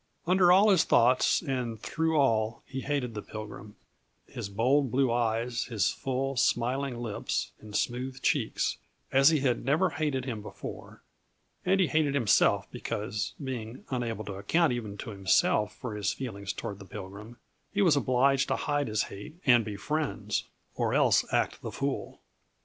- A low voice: Yes, low, 125 Hz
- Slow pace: No, average, 165 wpm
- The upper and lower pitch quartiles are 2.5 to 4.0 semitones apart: No, average, 4.6 semitones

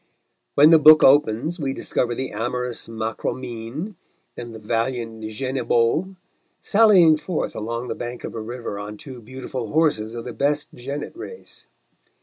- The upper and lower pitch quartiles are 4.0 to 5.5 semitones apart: Yes, average, 4.6 semitones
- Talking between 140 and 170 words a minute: Yes, average, 145 wpm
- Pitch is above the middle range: No, low, 125 Hz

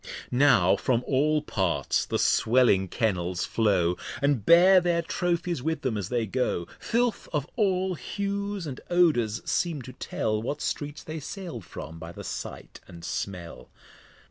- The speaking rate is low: No, average, 150 wpm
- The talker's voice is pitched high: No, low, 130 Hz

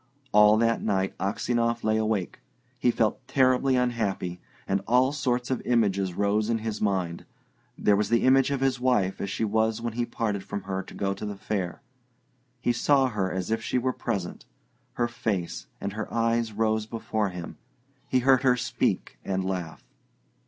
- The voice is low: Yes, low, 110 Hz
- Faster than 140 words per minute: Yes, average, 180 wpm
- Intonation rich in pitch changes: No, average, 3.6 semitones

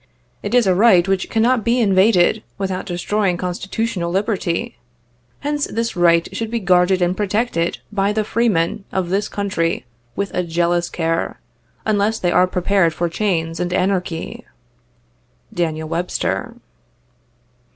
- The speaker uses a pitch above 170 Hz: Yes, medium, 185 Hz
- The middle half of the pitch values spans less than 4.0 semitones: Yes, average, 3.4 semitones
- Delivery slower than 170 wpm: Yes, average, 145 wpm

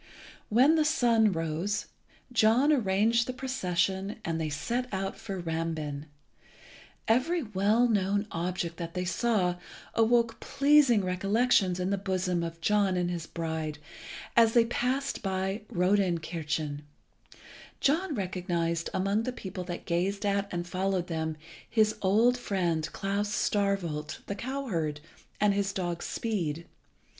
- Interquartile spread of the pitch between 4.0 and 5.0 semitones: Yes, average, 4.7 semitones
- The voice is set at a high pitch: Yes, high, 195 Hz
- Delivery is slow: Yes, slow, 130 wpm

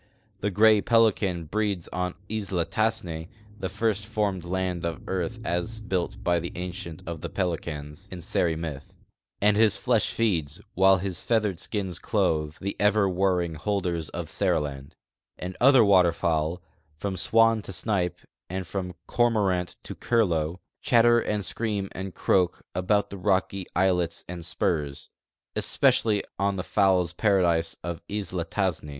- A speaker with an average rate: Yes, average, 150 wpm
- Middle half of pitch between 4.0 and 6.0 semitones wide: No, average, 3.4 semitones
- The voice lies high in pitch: No, very low, 95 Hz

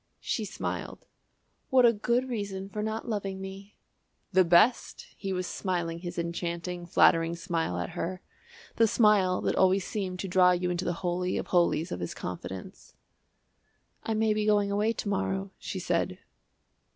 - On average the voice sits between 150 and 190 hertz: Yes, medium, 185 Hz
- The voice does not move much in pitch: No, average, 3.3 semitones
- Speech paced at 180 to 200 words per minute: No, average, 165 wpm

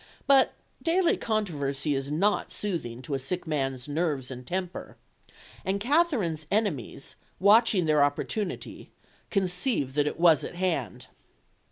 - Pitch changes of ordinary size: No, wide, 6.5 semitones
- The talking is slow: Yes, slow, 130 wpm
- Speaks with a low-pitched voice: No, medium, 170 Hz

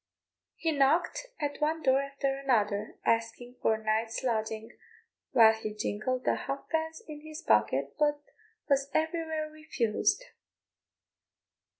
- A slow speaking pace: Yes, slow, 120 wpm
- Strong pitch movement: Yes, wide, 5.8 semitones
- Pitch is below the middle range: No, very high, 270 Hz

